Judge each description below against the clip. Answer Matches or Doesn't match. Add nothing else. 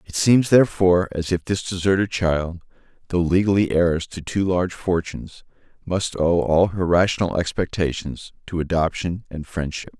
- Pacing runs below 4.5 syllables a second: Doesn't match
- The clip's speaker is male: Matches